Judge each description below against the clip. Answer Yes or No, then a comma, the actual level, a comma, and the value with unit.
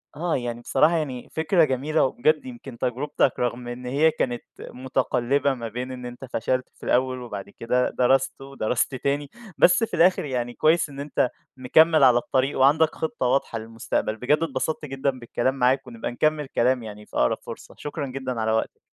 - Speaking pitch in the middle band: No, low, 130 Hz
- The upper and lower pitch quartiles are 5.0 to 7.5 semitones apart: No, average, 2.9 semitones